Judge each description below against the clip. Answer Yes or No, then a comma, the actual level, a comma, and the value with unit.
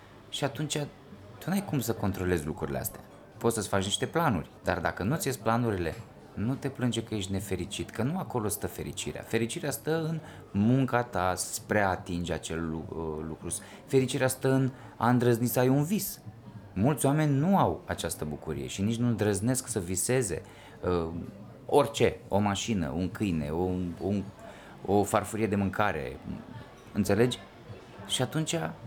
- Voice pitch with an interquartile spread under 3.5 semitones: No, average, 5.3 semitones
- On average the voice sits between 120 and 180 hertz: No, low, 110 Hz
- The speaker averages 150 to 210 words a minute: Yes, average, 160 wpm